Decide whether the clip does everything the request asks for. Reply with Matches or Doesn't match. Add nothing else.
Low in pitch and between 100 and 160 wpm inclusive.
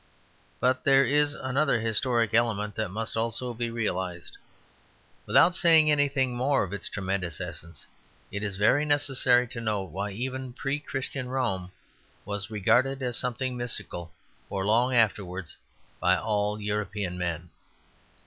Matches